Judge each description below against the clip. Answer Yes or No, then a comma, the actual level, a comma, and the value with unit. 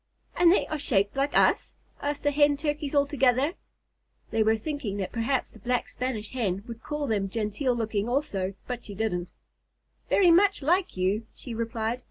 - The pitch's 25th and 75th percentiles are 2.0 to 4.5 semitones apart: No, average, 5.1 semitones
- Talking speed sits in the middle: Yes, average, 180 wpm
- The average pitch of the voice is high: Yes, high, 245 Hz